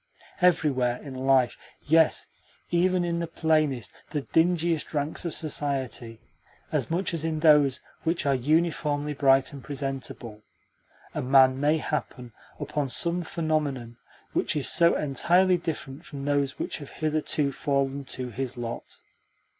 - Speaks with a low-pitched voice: No, medium, 145 Hz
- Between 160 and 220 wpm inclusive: No, average, 140 wpm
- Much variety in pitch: No, average, 3.3 semitones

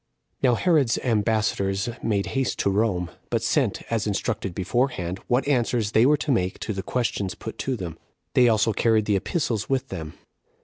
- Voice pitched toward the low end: Yes, low, 110 Hz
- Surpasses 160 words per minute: Yes, average, 180 wpm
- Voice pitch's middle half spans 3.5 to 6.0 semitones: Yes, average, 4.2 semitones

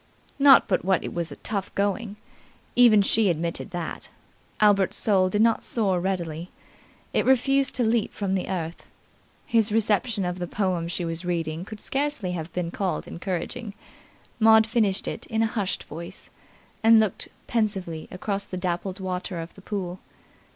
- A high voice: Yes, high, 195 Hz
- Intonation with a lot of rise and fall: No, average, 3.8 semitones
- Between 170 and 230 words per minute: No, average, 160 wpm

